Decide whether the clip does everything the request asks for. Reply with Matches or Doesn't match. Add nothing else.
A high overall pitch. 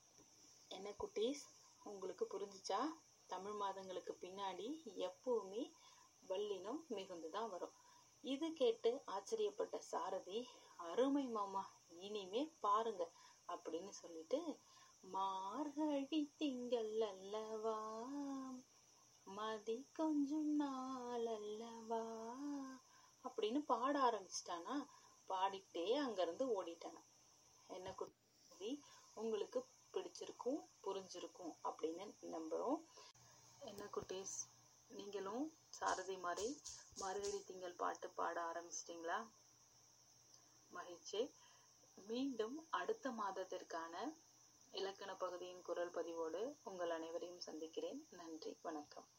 Matches